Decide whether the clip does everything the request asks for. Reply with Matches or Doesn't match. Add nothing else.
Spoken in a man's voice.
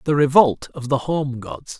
Matches